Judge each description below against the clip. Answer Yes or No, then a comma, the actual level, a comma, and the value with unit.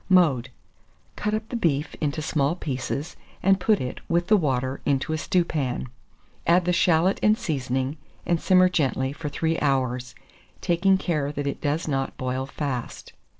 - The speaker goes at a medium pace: Yes, average, 160 wpm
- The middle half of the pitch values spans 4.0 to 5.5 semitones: Yes, average, 4.8 semitones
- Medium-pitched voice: Yes, medium, 150 Hz